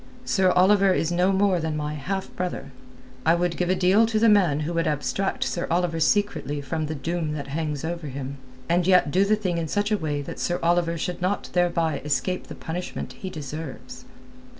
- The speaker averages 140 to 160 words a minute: No, fast, 205 wpm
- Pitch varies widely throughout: No, average, 3.5 semitones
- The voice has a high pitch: No, medium, 175 Hz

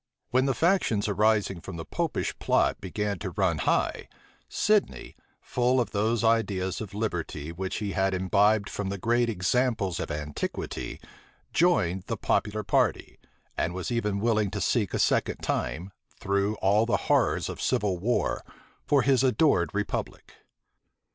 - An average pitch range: Yes, average, 3.7 semitones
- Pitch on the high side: No, low, 105 Hz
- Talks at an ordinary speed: Yes, average, 150 wpm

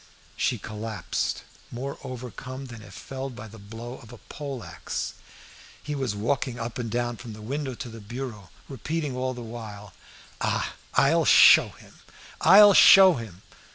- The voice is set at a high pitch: No, low, 120 Hz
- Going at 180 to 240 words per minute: No, average, 160 wpm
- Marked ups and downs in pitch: No, average, 3.2 semitones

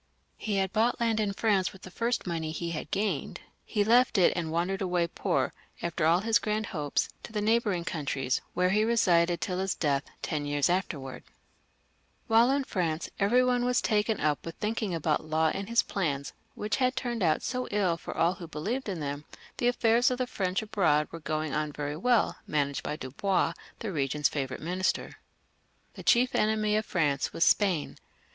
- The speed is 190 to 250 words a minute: Yes, average, 195 wpm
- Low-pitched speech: No, medium, 185 Hz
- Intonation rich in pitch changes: Yes, wide, 5.8 semitones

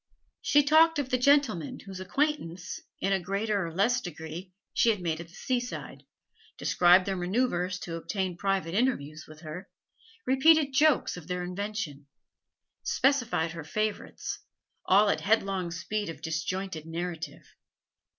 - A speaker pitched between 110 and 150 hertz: No, high, 190 Hz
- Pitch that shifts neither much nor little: No, wide, 6.1 semitones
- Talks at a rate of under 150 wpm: Yes, average, 140 wpm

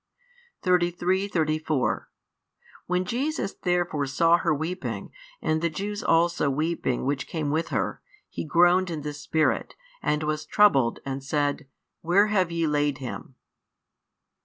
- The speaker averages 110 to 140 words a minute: Yes, slow, 135 wpm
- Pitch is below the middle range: No, medium, 160 Hz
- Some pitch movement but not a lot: Yes, average, 3.3 semitones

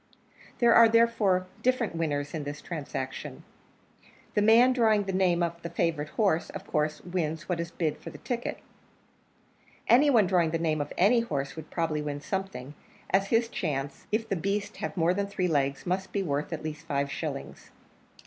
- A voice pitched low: No, medium, 175 Hz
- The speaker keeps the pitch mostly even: No, average, 5.0 semitones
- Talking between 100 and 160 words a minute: No, average, 185 wpm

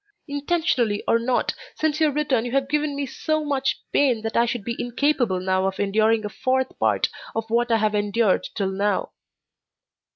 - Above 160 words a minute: Yes, average, 185 wpm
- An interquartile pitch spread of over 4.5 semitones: Yes, average, 4.9 semitones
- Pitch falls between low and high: No, high, 235 Hz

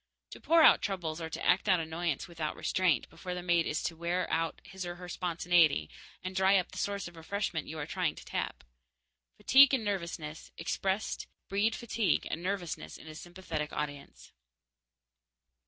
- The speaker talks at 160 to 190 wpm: Yes, average, 170 wpm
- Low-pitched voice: No, medium, 175 Hz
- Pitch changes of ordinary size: Yes, average, 3.0 semitones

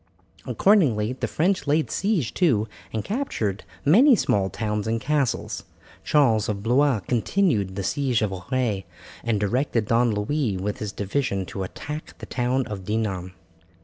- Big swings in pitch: Yes, wide, 5.8 semitones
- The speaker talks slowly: No, average, 145 wpm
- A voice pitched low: Yes, low, 115 Hz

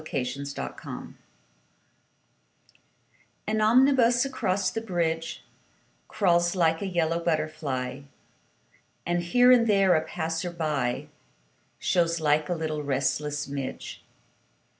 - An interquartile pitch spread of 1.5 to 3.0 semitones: No, average, 4.1 semitones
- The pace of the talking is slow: Yes, slow, 105 wpm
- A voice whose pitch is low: No, medium, 165 Hz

